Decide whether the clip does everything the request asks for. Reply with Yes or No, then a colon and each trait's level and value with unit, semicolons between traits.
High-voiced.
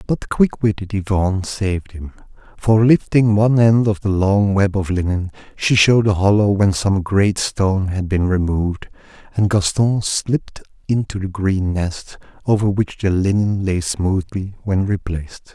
No: low, 100 Hz